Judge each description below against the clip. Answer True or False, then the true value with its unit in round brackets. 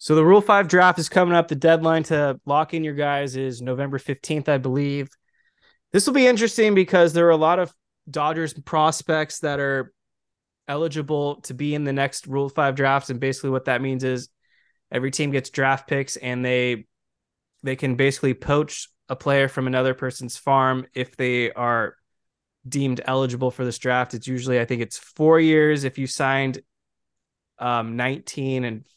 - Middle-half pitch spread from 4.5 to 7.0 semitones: False (3.2 semitones)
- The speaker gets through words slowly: False (180 wpm)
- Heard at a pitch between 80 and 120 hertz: False (135 Hz)